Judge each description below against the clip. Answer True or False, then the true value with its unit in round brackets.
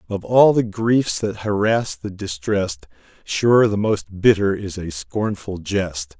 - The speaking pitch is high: False (105 Hz)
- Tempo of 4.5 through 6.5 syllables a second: False (3.6 syllables/s)